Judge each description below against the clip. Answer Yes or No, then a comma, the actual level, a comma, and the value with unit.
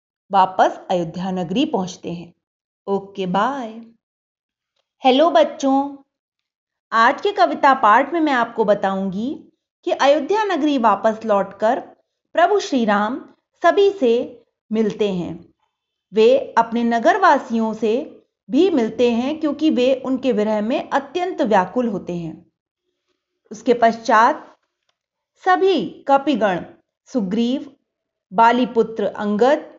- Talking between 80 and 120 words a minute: Yes, slow, 110 wpm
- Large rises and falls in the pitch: Yes, wide, 6.2 semitones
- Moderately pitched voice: No, high, 245 Hz